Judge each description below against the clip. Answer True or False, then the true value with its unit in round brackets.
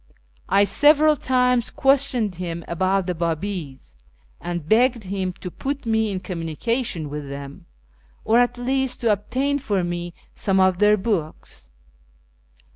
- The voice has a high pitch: True (200 Hz)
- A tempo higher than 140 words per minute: False (135 wpm)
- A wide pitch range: True (5.9 semitones)